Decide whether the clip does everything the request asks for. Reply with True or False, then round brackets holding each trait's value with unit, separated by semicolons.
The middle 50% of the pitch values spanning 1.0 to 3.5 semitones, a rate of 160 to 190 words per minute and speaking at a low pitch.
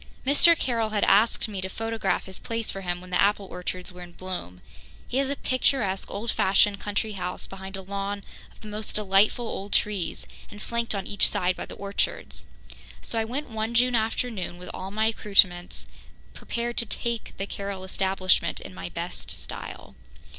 False (3.1 semitones; 185 wpm; 200 Hz)